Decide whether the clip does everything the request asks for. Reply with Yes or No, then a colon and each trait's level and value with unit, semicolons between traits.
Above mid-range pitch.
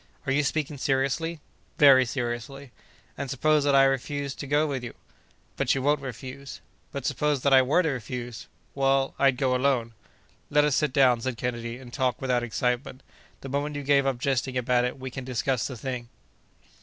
No: low, 135 Hz